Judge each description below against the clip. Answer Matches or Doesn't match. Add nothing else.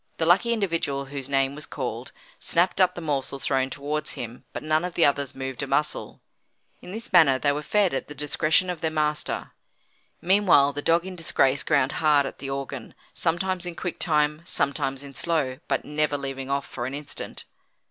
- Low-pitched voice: Doesn't match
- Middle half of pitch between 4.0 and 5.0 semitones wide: Doesn't match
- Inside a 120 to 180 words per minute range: Doesn't match